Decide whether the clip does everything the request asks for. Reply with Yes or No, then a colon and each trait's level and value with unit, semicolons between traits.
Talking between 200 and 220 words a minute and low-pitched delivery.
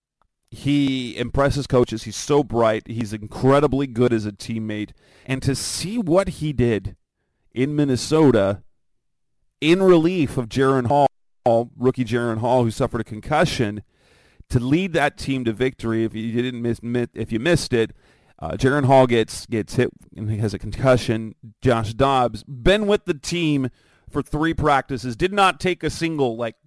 No: average, 160 wpm; low, 125 Hz